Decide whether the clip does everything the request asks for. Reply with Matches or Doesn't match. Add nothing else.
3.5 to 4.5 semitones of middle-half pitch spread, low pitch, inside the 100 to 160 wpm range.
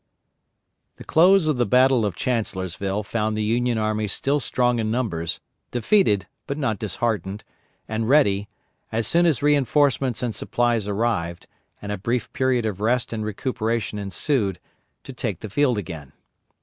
Matches